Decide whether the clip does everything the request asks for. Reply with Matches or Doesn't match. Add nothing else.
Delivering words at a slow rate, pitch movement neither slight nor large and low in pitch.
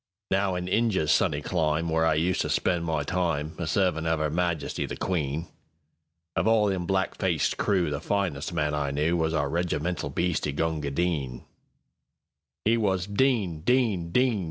Doesn't match